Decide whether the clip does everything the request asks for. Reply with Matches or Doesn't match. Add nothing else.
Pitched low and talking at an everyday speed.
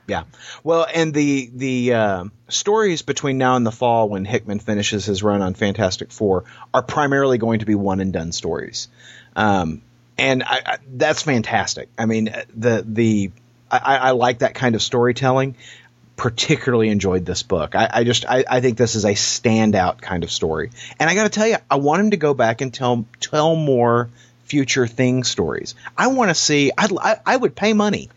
Matches